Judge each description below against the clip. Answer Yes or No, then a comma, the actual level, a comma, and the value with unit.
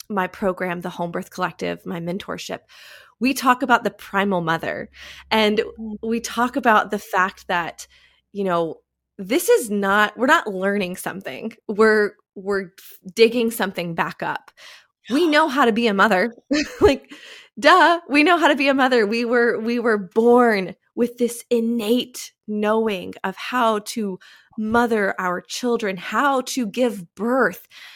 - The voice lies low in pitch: No, high, 220 Hz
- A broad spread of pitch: No, average, 3.9 semitones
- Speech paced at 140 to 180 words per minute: Yes, average, 150 wpm